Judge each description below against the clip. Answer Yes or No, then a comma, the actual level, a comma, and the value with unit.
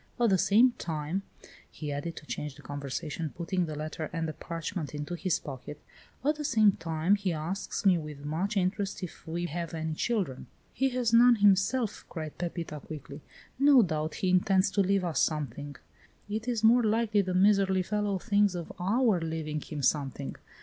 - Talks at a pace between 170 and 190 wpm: Yes, average, 180 wpm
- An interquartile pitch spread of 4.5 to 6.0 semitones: Yes, average, 4.8 semitones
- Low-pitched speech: No, medium, 180 Hz